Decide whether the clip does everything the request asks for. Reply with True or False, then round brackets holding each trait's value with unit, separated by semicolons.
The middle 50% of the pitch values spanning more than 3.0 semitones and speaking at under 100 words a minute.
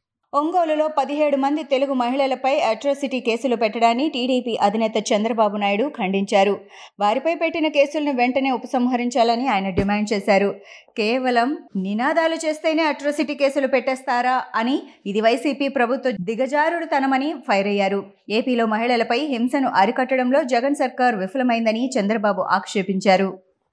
False (4.4 semitones; 110 wpm)